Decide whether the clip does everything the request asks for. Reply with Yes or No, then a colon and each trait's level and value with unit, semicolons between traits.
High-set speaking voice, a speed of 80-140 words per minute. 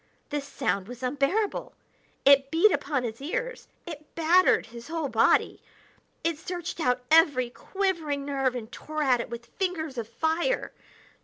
No: very high, 290 Hz; average, 150 wpm